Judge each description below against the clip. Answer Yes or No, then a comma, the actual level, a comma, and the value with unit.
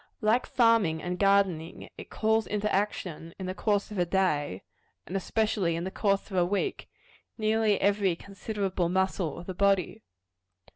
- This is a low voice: No, high, 195 Hz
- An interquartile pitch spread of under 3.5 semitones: Yes, average, 2.9 semitones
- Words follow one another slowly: No, average, 160 wpm